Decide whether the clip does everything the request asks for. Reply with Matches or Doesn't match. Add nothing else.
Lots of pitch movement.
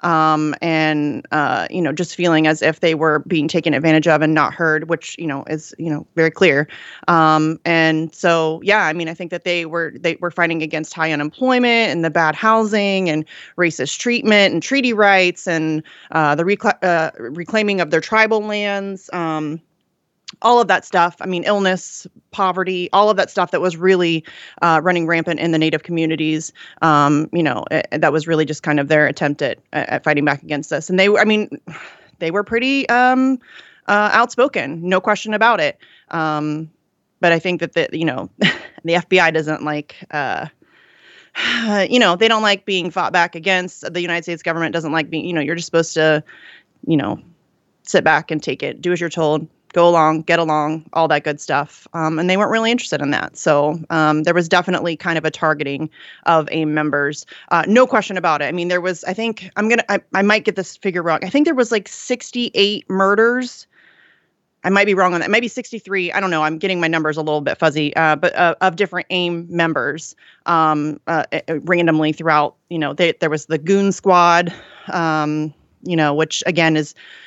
Doesn't match